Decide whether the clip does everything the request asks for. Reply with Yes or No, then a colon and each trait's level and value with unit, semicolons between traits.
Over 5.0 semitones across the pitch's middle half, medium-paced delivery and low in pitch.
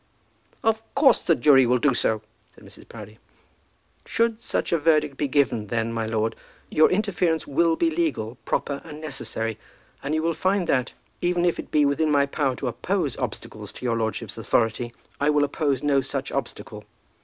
No: wide, 5.4 semitones; average, 180 wpm; medium, 145 Hz